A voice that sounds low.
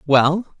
No: medium, 160 Hz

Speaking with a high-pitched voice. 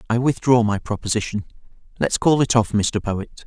No: low, 115 Hz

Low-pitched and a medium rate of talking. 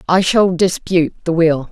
No: medium, 175 Hz; average, 175 wpm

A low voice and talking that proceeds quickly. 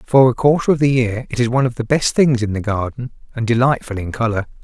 Yes: low, 120 Hz; fast, 260 wpm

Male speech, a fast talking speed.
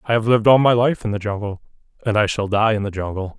Yes: male; fast, 285 wpm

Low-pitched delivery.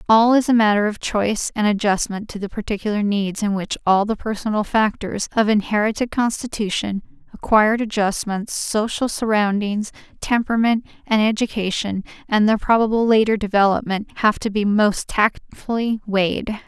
No: high, 210 Hz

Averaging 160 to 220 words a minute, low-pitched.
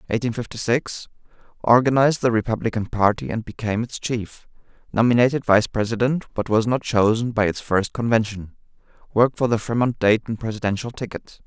No: average, 145 wpm; low, 115 Hz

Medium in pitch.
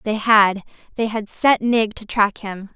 No: high, 215 Hz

